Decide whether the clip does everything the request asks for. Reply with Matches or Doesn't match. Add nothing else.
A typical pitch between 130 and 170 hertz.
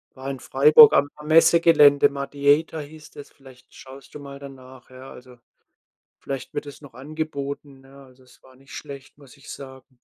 Matches